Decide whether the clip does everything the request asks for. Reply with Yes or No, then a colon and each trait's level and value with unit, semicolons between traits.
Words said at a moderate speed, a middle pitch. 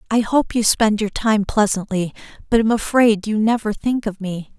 No: average, 195 wpm; high, 215 Hz